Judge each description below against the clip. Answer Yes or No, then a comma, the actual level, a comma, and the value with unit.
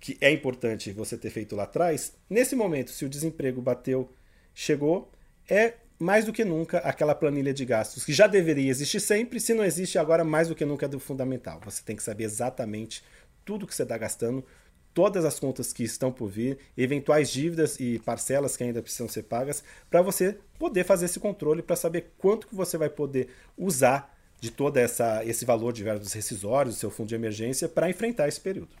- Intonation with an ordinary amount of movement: No, wide, 6.3 semitones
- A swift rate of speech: Yes, fast, 200 wpm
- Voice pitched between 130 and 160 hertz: Yes, medium, 140 Hz